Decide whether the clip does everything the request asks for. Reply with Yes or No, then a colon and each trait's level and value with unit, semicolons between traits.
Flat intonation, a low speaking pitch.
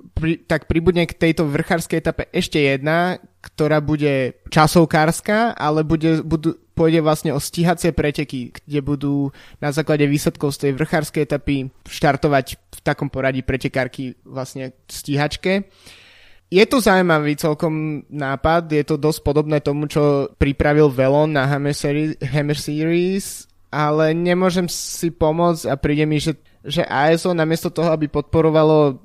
No: narrow, 2.3 semitones; medium, 150 Hz